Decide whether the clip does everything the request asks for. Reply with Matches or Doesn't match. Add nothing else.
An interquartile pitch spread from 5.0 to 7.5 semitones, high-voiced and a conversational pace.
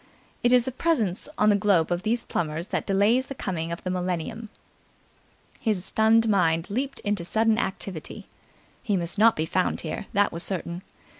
Doesn't match